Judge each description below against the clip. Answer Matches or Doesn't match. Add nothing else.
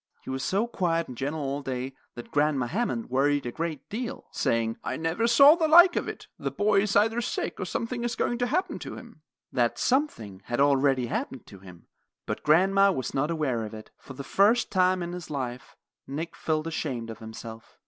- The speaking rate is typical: Doesn't match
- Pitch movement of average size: Doesn't match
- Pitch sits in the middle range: Matches